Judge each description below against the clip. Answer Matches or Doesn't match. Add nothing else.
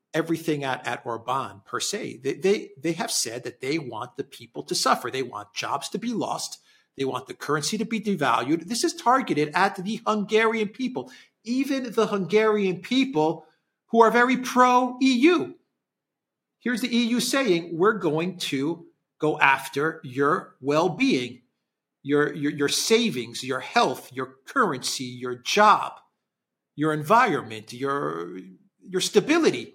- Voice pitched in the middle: Matches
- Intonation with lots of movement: Matches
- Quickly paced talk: Doesn't match